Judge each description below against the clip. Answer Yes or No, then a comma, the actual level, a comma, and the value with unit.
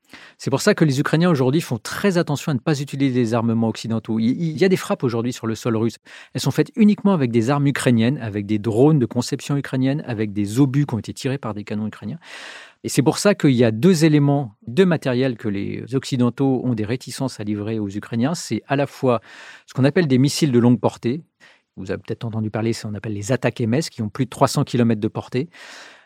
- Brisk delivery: Yes, fast, 240 wpm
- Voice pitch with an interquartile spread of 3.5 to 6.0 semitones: Yes, average, 4.2 semitones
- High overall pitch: No, low, 125 Hz